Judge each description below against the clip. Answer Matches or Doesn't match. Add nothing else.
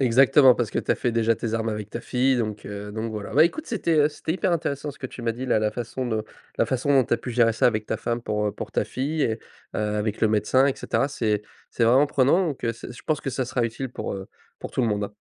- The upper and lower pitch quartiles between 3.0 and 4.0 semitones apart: Matches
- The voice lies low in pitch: Matches